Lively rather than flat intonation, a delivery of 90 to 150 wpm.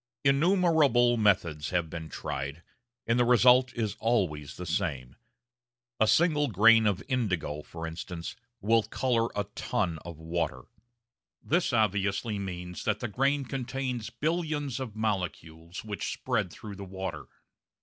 Yes: wide, 6.3 semitones; slow, 135 wpm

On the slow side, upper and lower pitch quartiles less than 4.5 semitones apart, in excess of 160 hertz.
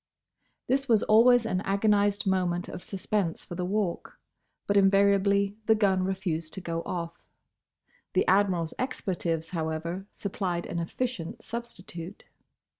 Yes: slow, 125 wpm; average, 3.0 semitones; high, 190 Hz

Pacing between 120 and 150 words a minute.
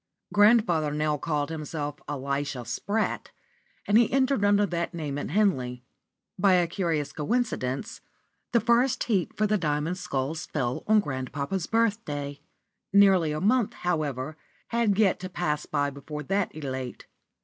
Yes: average, 140 wpm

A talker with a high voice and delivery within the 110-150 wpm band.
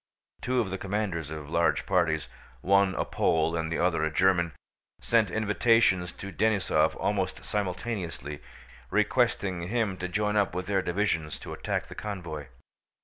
No: very low, 95 Hz; average, 145 wpm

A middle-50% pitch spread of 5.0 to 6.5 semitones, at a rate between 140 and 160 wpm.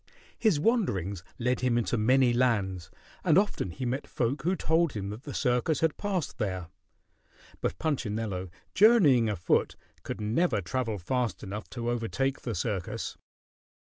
Yes: wide, 5.6 semitones; average, 145 wpm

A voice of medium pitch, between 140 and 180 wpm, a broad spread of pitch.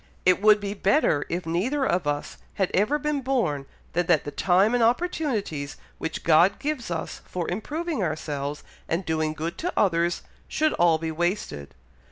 Yes: medium, 180 Hz; average, 170 wpm; wide, 6.9 semitones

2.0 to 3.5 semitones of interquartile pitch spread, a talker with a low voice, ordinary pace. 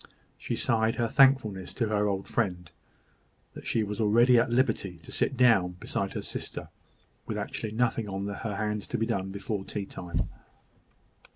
Yes: average, 3.1 semitones; low, 105 Hz; average, 170 wpm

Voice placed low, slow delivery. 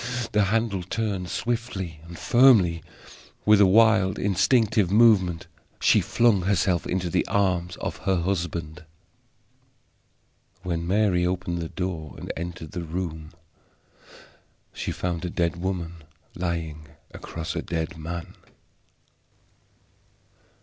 Yes: very low, 90 Hz; slow, 115 wpm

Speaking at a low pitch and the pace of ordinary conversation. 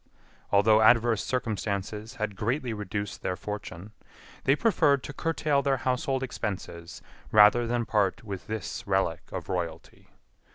No: low, 110 Hz; slow, 130 wpm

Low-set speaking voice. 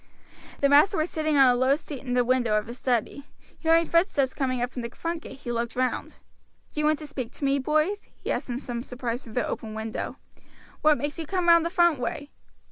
No: very high, 275 Hz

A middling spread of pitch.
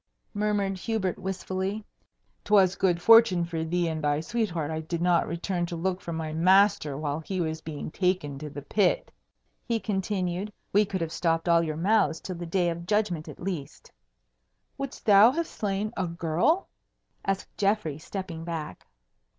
Yes: average, 3.5 semitones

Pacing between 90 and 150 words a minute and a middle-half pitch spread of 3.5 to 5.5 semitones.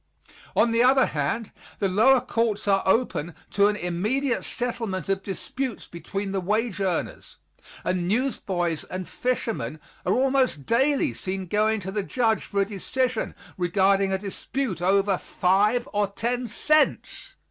Yes: average, 145 wpm; average, 4.3 semitones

